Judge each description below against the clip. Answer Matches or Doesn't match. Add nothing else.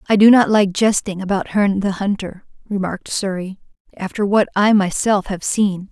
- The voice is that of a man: Doesn't match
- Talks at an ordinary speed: Matches